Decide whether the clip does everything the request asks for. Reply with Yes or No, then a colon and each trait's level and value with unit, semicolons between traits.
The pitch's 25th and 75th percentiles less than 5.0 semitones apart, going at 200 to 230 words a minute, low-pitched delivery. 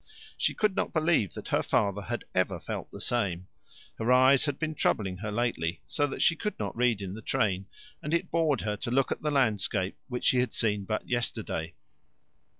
No: wide, 5.4 semitones; fast, 205 wpm; low, 120 Hz